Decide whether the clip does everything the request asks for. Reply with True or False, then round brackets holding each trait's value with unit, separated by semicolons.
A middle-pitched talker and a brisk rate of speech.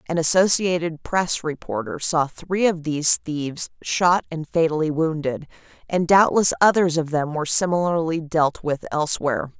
False (160 Hz; 145 wpm)